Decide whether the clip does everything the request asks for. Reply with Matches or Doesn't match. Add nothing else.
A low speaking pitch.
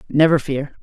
Doesn't match